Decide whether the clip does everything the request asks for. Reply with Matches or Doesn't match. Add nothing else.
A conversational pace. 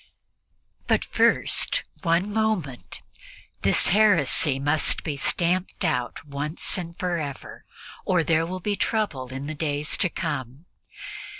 Doesn't match